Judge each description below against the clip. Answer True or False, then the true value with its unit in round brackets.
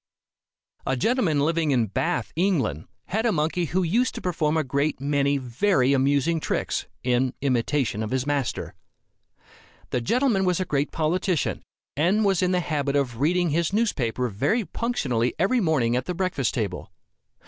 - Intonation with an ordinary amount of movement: False (5.8 semitones)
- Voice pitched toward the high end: False (150 Hz)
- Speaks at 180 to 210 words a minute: False (160 wpm)